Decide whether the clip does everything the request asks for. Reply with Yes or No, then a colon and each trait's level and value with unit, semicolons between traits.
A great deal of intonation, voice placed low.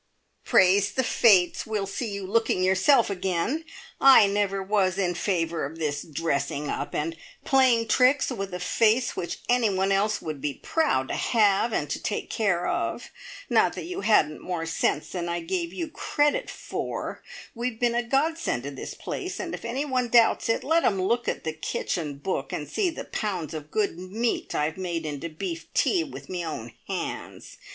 No: wide, 6.4 semitones; high, 195 Hz